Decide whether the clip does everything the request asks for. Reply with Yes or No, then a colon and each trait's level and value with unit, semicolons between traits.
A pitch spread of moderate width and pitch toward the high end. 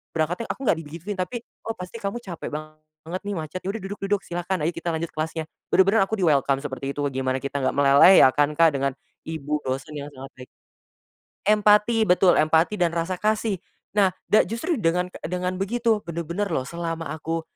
No: average, 4.4 semitones; medium, 170 Hz